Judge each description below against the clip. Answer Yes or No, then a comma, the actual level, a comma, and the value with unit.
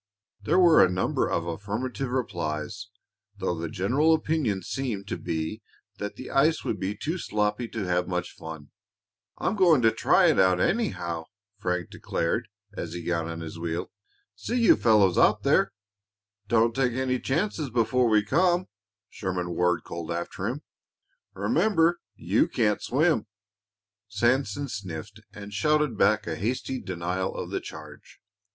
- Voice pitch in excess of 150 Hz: No, low, 105 Hz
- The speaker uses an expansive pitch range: Yes, wide, 6.8 semitones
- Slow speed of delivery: No, average, 150 wpm